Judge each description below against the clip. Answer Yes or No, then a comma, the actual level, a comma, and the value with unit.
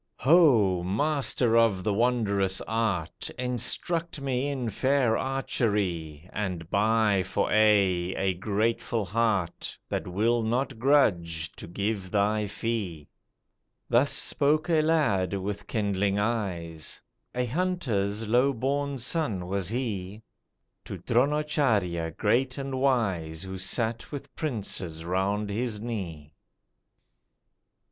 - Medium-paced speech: No, slow, 110 wpm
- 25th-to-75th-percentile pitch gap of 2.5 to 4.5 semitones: No, average, 5.0 semitones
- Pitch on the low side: Yes, low, 110 Hz